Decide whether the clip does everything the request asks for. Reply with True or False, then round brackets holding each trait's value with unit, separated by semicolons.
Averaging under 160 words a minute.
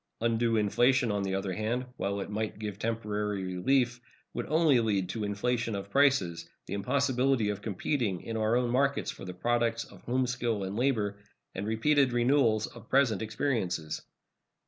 False (170 wpm)